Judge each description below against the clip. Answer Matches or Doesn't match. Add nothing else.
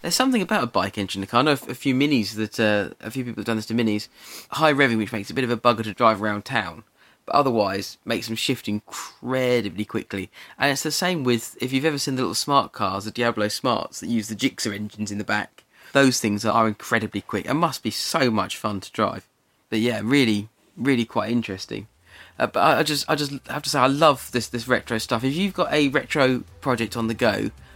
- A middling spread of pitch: Matches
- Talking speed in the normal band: Doesn't match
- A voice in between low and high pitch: Doesn't match